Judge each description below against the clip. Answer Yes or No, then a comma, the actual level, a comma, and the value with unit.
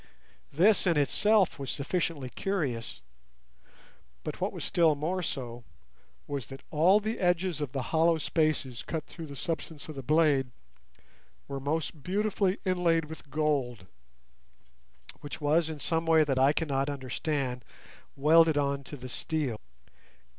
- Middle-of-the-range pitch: Yes, medium, 150 Hz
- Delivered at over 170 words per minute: No, average, 140 wpm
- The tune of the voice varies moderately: Yes, average, 3.3 semitones